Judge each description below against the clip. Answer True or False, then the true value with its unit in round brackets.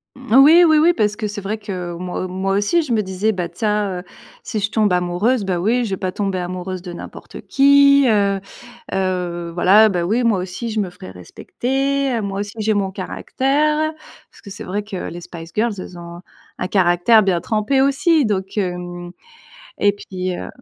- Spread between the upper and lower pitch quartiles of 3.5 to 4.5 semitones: True (4.2 semitones)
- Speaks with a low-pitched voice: False (200 Hz)